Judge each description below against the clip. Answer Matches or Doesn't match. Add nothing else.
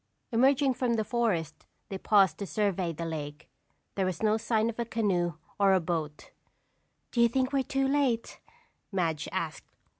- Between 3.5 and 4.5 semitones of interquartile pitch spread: Doesn't match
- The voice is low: Doesn't match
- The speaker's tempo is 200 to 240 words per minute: Doesn't match